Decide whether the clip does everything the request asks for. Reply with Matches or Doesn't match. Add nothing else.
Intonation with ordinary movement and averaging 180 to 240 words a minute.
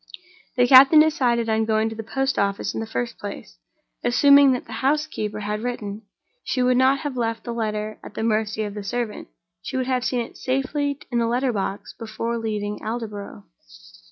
Matches